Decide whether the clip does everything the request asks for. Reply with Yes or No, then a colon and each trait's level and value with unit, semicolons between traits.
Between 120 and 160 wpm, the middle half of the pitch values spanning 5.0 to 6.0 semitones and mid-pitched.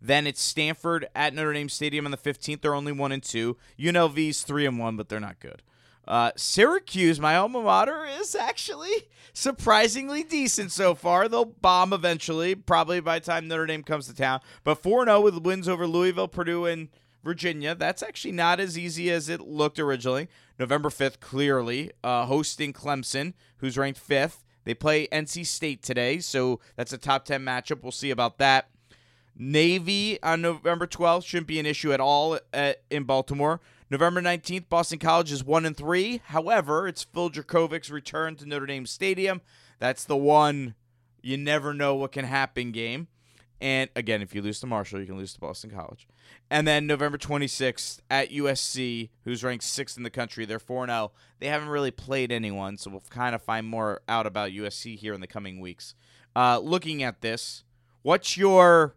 No: average, 180 wpm; wide, 5.4 semitones; medium, 145 Hz